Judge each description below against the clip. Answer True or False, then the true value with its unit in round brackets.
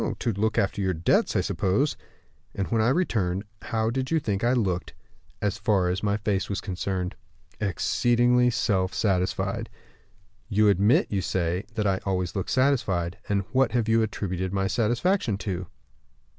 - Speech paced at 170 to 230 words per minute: False (160 wpm)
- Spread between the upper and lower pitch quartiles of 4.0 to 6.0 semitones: False (3.6 semitones)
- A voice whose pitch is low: True (100 Hz)